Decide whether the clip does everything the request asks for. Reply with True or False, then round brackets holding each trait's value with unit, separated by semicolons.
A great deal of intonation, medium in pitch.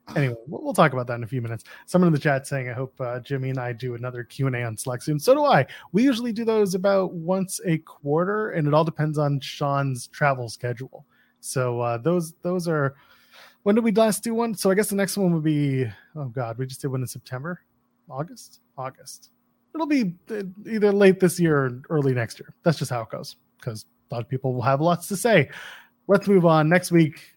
True (6.5 semitones; 150 Hz)